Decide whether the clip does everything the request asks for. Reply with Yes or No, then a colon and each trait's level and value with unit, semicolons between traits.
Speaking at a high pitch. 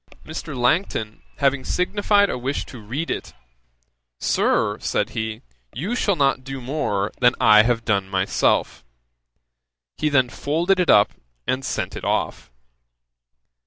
No: low, 130 Hz